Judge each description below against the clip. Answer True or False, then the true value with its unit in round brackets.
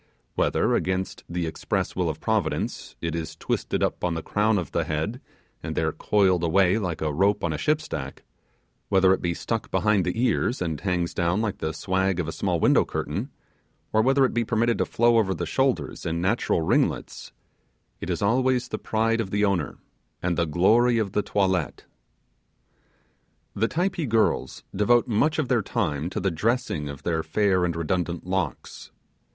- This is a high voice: False (95 Hz)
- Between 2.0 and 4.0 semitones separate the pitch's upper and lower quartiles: False (4.9 semitones)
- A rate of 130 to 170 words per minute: False (180 wpm)